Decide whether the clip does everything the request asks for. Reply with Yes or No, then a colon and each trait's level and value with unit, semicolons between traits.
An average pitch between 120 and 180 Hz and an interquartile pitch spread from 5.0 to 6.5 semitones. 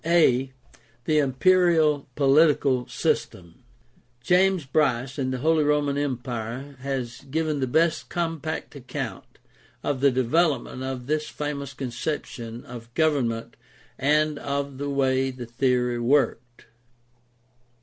No: medium, 140 Hz; average, 3.4 semitones